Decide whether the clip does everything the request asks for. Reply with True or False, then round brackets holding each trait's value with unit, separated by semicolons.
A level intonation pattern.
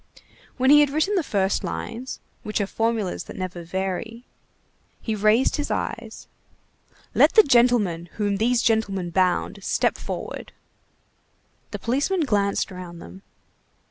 False (4.6 semitones)